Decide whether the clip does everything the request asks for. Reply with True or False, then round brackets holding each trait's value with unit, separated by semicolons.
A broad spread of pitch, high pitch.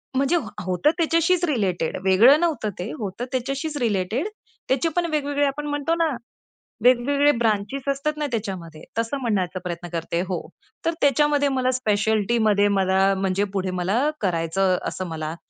True (7.2 semitones; 230 Hz)